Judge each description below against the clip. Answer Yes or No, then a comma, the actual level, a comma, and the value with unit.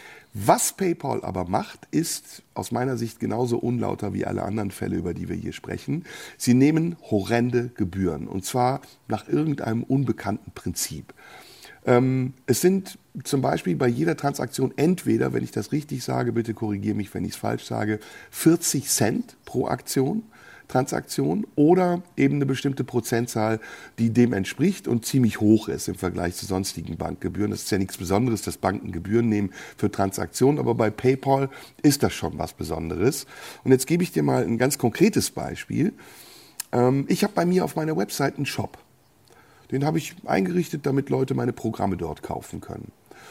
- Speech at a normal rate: Yes, average, 170 wpm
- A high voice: No, low, 120 Hz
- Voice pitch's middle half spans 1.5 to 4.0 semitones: No, average, 4.7 semitones